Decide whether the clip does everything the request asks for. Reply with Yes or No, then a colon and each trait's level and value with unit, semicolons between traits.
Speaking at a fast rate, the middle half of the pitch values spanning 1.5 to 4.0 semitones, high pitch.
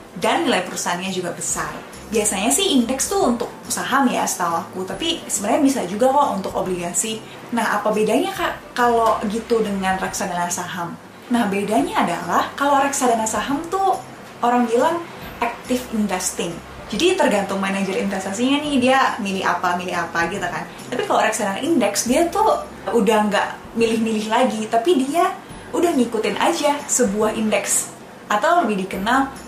No: fast, 150 wpm; wide, 5.4 semitones; high, 225 Hz